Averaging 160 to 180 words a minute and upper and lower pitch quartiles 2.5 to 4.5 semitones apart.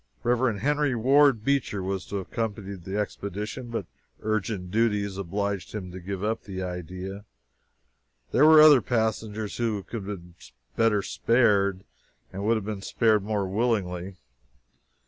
No: average, 145 wpm; average, 3.0 semitones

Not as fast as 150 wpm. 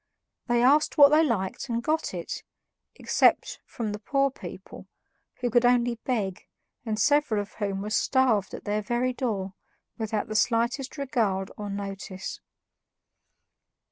Yes: average, 140 wpm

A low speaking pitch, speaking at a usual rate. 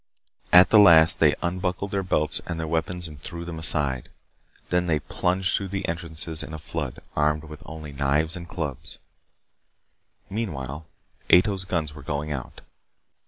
Yes: very low, 80 Hz; average, 160 wpm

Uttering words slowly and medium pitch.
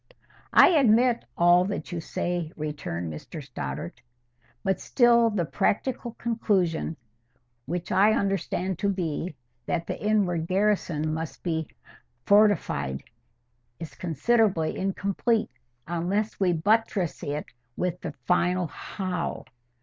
Yes: slow, 105 wpm; medium, 175 Hz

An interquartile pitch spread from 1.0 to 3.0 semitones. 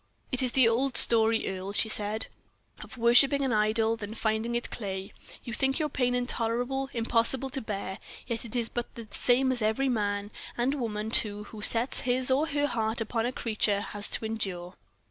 Yes: average, 2.7 semitones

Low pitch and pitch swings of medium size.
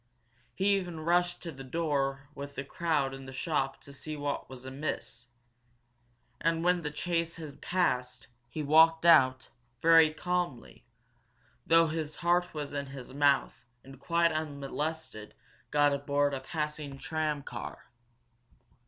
No: medium, 150 Hz; average, 3.3 semitones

